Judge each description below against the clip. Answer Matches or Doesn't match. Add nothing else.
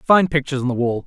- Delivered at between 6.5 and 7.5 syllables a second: Matches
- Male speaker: Matches